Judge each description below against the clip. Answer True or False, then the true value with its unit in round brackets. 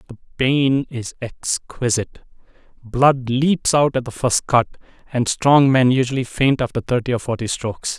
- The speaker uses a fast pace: False (160 wpm)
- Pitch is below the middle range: True (125 Hz)